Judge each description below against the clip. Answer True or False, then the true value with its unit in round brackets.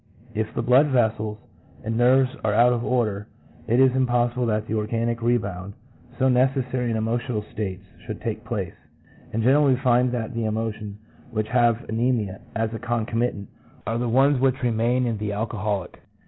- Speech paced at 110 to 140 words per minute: False (175 wpm)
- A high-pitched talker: False (115 Hz)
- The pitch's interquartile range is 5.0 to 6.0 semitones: False (2.4 semitones)